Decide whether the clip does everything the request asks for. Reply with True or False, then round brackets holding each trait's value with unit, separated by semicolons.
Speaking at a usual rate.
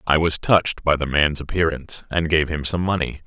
False (220 wpm)